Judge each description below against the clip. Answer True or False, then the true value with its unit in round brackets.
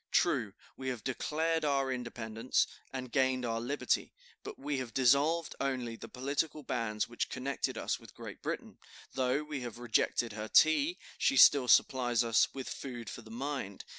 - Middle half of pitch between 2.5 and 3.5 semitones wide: True (2.9 semitones)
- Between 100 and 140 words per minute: False (165 wpm)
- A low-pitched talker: True (130 Hz)